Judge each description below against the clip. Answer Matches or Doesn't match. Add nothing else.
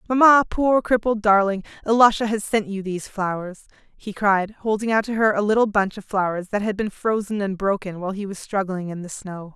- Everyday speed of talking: Doesn't match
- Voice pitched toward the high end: Matches